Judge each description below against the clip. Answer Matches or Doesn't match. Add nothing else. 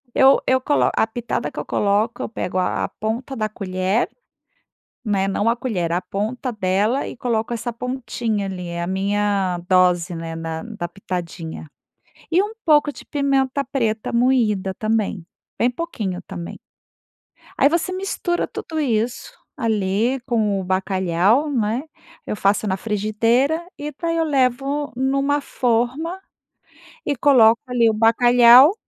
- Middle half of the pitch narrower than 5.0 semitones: Doesn't match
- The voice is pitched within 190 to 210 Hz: Doesn't match